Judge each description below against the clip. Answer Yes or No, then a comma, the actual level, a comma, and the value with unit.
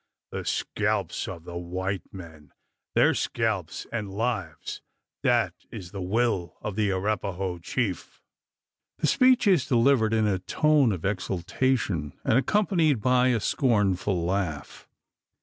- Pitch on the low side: Yes, low, 100 Hz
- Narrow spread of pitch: No, wide, 5.5 semitones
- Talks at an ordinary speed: No, slow, 130 wpm